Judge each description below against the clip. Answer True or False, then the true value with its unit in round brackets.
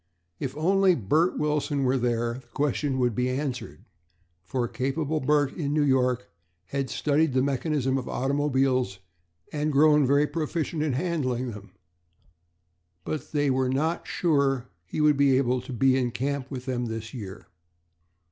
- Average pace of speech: True (155 wpm)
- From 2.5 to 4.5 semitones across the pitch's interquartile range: True (2.8 semitones)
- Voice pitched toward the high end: False (135 Hz)